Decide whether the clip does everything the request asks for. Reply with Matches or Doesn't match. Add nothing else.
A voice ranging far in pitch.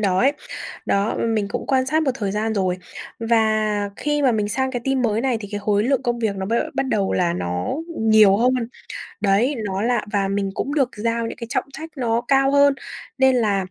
Doesn't match